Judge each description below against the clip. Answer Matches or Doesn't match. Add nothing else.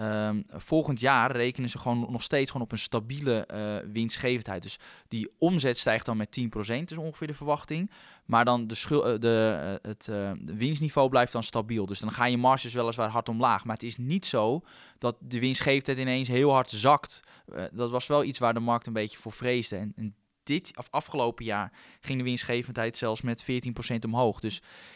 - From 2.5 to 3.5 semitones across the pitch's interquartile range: Matches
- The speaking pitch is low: Matches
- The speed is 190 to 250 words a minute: Matches